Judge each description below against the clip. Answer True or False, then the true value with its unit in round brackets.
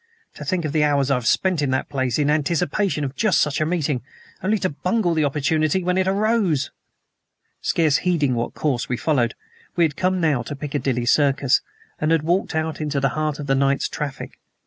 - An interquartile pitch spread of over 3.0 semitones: True (3.8 semitones)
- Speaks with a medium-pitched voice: True (150 Hz)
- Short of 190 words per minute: False (205 wpm)